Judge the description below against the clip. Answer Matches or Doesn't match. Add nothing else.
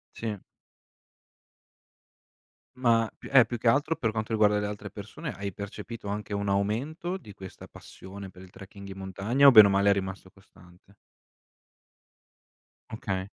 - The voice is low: Matches